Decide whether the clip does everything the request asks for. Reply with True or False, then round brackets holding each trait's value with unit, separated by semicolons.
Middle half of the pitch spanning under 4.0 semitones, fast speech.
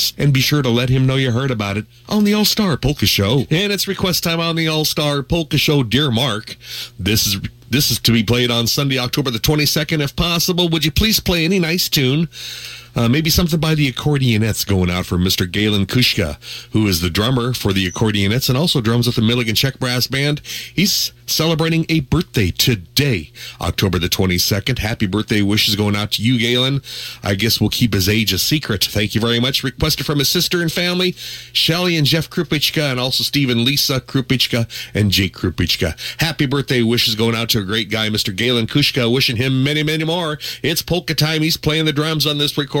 False (5.5 semitones; 210 wpm)